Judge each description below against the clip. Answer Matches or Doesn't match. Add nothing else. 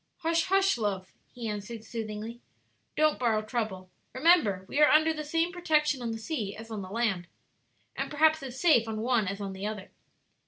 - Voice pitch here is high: Matches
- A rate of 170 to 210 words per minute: Matches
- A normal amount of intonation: Doesn't match